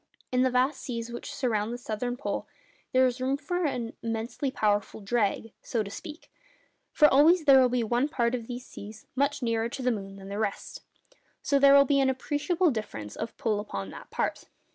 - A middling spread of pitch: Yes, average, 4.0 semitones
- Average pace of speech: No, fast, 210 wpm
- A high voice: Yes, high, 245 Hz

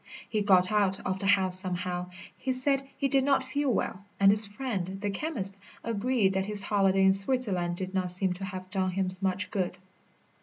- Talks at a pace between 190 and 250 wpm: Yes, average, 195 wpm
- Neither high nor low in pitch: No, high, 195 Hz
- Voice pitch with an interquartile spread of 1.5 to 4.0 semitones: Yes, average, 2.8 semitones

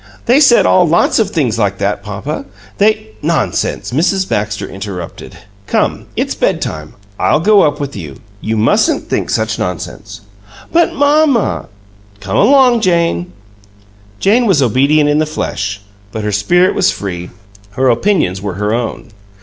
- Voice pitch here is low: Yes, low, 125 Hz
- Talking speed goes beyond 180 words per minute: No, average, 160 wpm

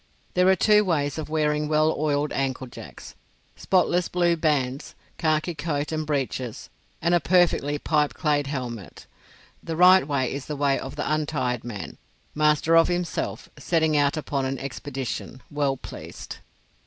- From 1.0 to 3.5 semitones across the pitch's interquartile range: Yes, average, 3.0 semitones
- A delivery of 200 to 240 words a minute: No, average, 150 wpm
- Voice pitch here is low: No, medium, 150 Hz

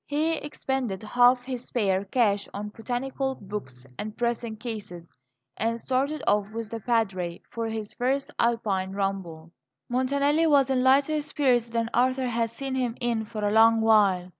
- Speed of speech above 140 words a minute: Yes, average, 160 wpm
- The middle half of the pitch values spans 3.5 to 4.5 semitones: Yes, average, 3.8 semitones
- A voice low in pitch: No, high, 230 Hz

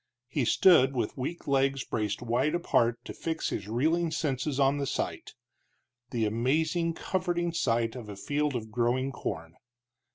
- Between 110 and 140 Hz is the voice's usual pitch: Yes, low, 135 Hz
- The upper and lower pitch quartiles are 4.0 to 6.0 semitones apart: Yes, average, 5.2 semitones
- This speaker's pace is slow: No, average, 155 wpm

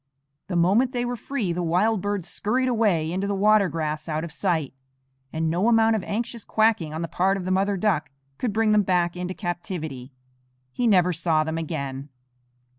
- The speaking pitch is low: No, medium, 185 Hz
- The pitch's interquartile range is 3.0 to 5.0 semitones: Yes, average, 4.7 semitones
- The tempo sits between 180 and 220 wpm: Yes, average, 190 wpm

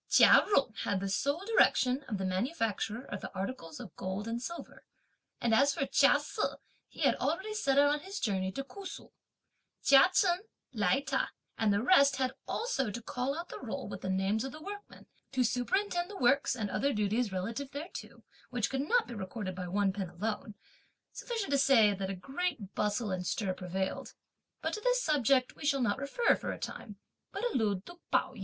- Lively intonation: Yes, wide, 6.1 semitones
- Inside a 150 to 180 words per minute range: No, fast, 205 wpm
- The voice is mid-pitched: No, very high, 250 Hz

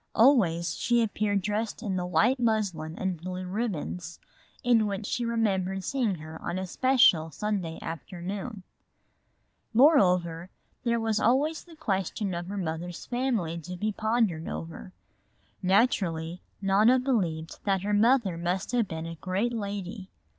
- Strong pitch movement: No, average, 4.6 semitones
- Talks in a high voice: Yes, high, 195 Hz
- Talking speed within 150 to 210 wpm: No, average, 140 wpm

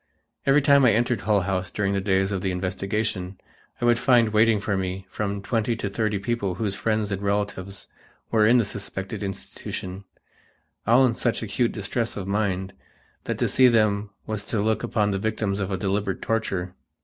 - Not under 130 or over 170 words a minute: No, average, 185 wpm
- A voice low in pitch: Yes, low, 105 Hz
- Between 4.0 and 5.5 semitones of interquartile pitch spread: No, narrow, 2.6 semitones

